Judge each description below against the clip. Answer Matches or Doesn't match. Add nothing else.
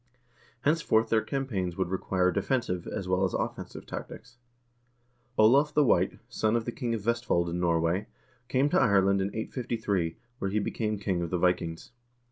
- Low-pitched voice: Matches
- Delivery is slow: Doesn't match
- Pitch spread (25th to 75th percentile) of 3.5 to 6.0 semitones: Matches